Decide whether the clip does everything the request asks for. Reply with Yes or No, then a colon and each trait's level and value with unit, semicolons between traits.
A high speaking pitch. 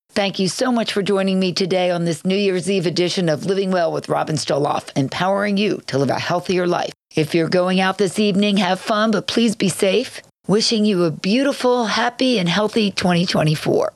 Yes: high, 195 Hz